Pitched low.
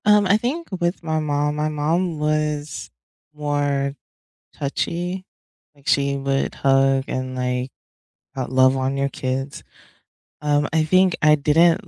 No: medium, 145 Hz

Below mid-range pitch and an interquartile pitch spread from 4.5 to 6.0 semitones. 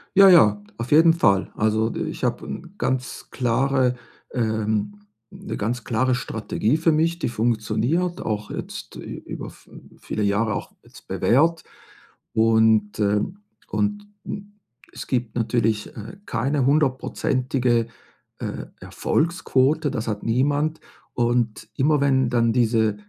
Yes: low, 125 Hz; average, 5.2 semitones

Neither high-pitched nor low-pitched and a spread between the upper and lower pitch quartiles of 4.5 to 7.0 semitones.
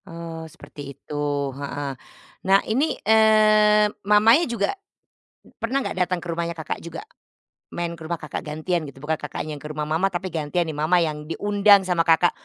Yes: medium, 170 Hz; average, 5.1 semitones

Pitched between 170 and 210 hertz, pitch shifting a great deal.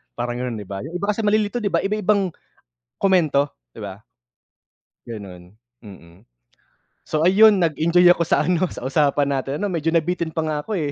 No: medium, 160 Hz; wide, 6.8 semitones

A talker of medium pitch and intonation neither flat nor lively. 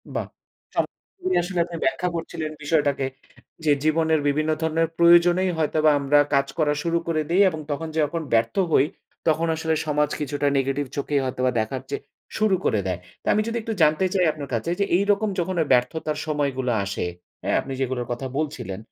Yes: medium, 155 Hz; average, 3.7 semitones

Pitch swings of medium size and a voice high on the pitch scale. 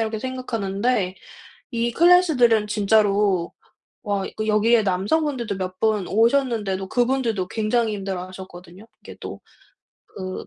Yes: average, 3.7 semitones; high, 215 Hz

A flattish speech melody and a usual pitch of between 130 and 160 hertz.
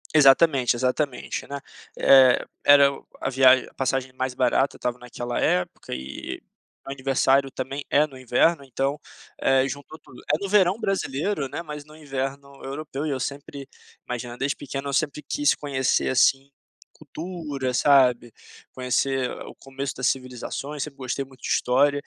Yes: narrow, 1.8 semitones; low, 135 Hz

